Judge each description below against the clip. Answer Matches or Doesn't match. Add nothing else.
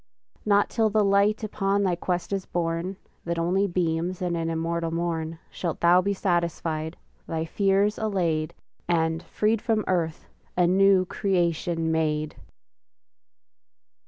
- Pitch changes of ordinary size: Matches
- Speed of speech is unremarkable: Doesn't match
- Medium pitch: Matches